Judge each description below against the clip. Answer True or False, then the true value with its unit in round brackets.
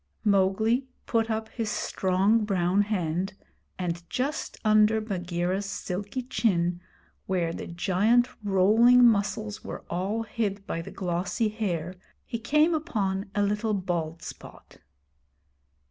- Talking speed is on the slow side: True (120 wpm)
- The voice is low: False (200 Hz)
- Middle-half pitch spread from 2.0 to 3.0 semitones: False (3.5 semitones)